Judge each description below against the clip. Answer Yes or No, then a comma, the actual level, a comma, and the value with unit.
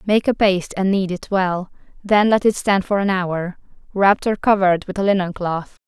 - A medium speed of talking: No, fast, 215 wpm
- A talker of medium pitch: No, high, 195 Hz